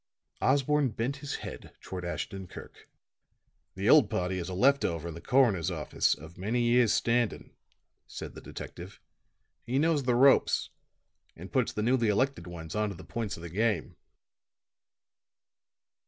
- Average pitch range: No, wide, 6.2 semitones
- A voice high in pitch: No, low, 110 Hz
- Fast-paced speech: No, average, 155 wpm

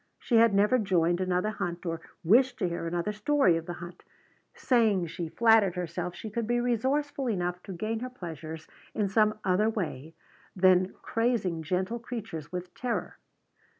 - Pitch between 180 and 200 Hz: Yes, high, 190 Hz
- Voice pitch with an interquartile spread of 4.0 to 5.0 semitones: Yes, average, 4.6 semitones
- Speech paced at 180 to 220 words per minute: No, average, 165 wpm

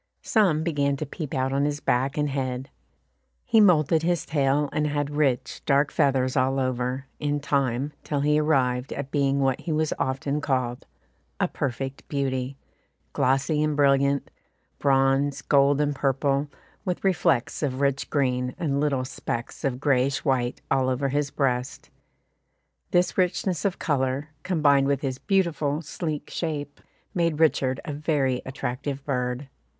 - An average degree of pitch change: No, narrow, 2.1 semitones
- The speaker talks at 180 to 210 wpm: No, average, 150 wpm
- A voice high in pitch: No, medium, 140 Hz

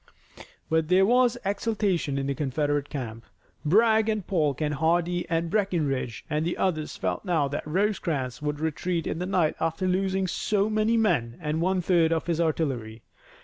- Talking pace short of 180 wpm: Yes, average, 170 wpm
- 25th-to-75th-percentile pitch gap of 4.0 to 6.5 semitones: Yes, average, 4.4 semitones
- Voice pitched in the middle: Yes, medium, 165 Hz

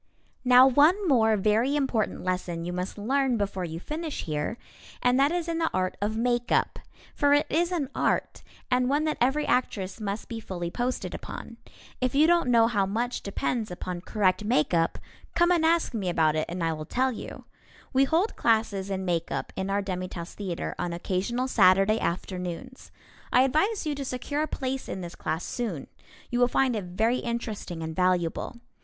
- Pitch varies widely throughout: Yes, wide, 6.4 semitones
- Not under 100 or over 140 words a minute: No, average, 185 wpm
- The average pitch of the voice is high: Yes, high, 225 Hz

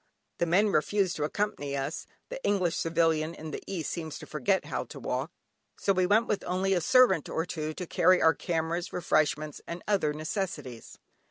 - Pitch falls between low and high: Yes, medium, 170 Hz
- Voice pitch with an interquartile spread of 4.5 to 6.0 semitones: No, average, 3.8 semitones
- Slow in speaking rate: No, average, 185 wpm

